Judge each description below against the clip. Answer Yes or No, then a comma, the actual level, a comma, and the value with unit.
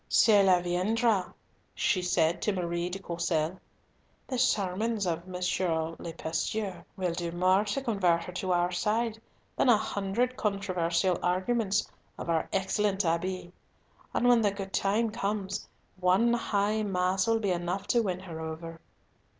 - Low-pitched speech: No, high, 190 Hz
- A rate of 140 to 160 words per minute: Yes, average, 150 wpm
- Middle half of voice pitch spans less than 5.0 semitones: Yes, average, 3.1 semitones